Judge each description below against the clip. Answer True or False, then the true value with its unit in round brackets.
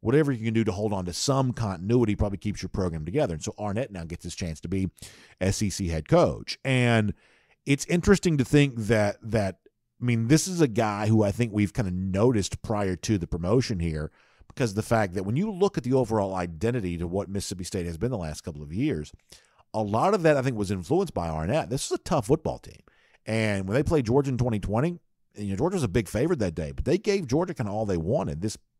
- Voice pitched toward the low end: True (110 Hz)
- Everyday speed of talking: False (245 wpm)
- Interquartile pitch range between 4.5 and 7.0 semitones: True (5.0 semitones)